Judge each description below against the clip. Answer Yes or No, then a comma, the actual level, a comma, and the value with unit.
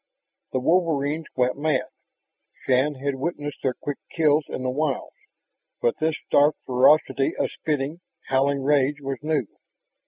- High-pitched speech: No, medium, 145 Hz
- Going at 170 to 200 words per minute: No, slow, 135 wpm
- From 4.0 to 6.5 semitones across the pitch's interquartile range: No, narrow, 2.4 semitones